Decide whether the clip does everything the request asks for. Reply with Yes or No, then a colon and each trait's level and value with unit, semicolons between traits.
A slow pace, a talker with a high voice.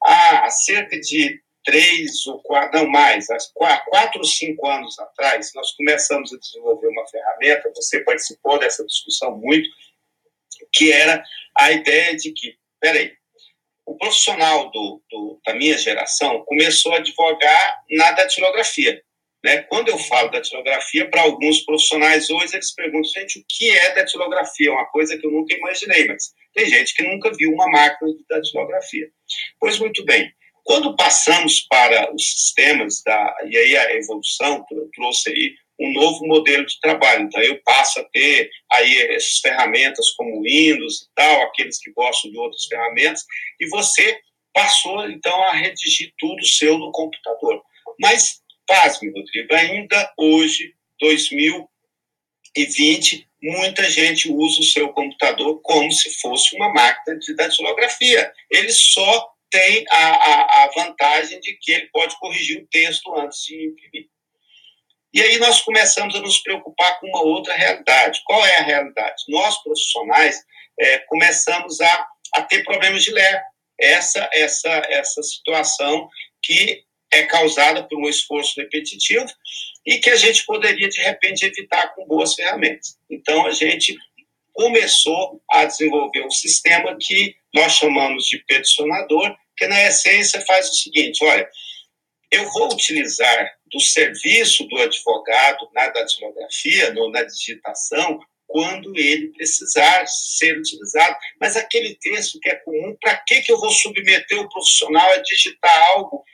No: average, 150 wpm; high, 195 Hz